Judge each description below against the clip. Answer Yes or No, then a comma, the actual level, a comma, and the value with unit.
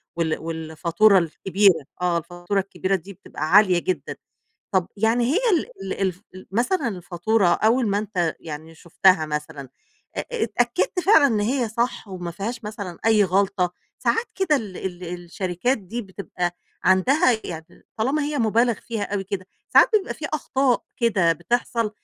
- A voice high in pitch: Yes, high, 195 Hz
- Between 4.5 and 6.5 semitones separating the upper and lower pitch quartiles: Yes, average, 4.9 semitones